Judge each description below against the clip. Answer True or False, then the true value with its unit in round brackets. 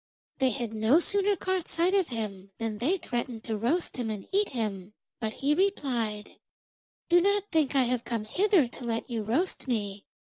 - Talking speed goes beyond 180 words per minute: True (190 wpm)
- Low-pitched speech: False (245 Hz)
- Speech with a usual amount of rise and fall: False (8.0 semitones)